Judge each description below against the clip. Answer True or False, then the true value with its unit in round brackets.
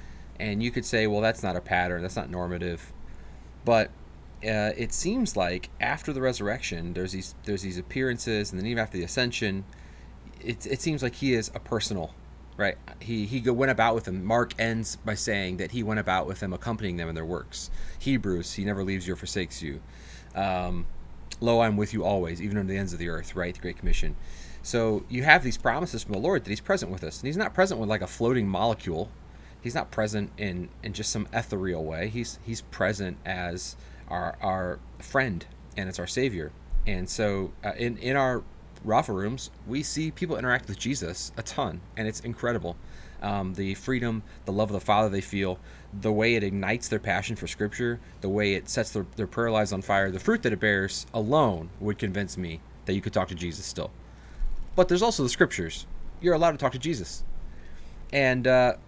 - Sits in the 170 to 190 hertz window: False (100 Hz)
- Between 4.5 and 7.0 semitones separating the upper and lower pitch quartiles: True (4.9 semitones)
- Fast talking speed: True (210 wpm)